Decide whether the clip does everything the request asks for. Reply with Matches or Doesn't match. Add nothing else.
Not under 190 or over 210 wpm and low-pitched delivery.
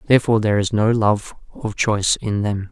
Matches